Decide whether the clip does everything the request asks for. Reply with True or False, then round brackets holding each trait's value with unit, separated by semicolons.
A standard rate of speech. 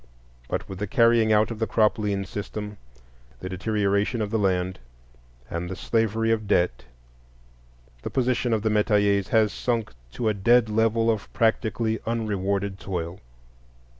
True (150 wpm)